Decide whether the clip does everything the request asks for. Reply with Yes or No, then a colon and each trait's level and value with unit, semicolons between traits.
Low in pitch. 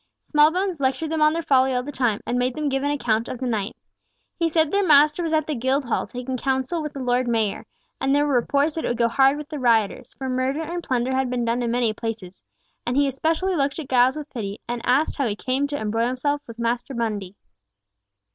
No: very high, 265 Hz